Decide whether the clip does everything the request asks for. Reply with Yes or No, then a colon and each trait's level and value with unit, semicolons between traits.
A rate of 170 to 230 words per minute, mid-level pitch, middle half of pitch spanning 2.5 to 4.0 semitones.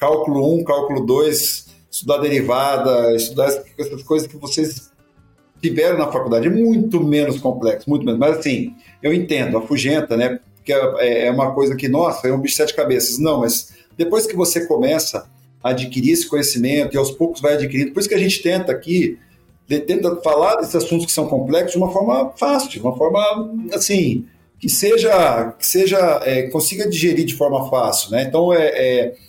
No: fast, 185 wpm; medium, 145 Hz; average, 4.5 semitones